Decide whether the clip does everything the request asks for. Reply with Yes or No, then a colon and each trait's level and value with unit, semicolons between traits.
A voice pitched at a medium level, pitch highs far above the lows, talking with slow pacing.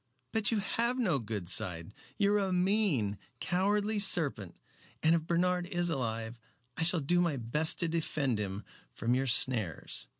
No: medium, 160 Hz; wide, 8.5 semitones; average, 165 wpm